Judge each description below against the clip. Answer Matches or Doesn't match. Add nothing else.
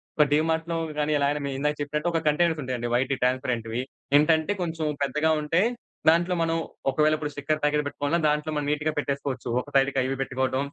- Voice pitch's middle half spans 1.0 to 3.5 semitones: Matches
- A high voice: Doesn't match